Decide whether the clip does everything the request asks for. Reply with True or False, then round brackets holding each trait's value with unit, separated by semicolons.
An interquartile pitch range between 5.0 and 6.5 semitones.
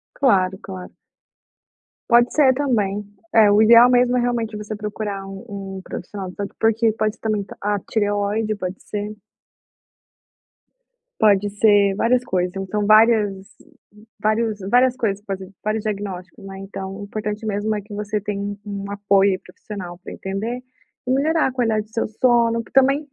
False (2.4 semitones)